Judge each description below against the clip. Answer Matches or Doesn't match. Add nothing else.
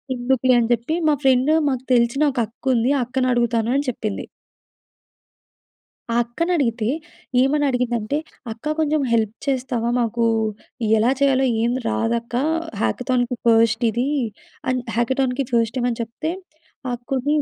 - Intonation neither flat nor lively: Doesn't match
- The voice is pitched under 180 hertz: Doesn't match